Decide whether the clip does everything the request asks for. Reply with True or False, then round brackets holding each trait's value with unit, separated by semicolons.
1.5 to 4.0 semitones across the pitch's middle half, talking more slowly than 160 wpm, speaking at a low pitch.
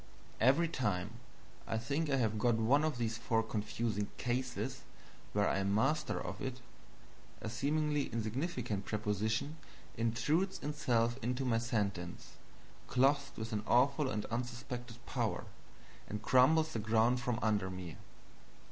True (3.6 semitones; 135 wpm; 120 Hz)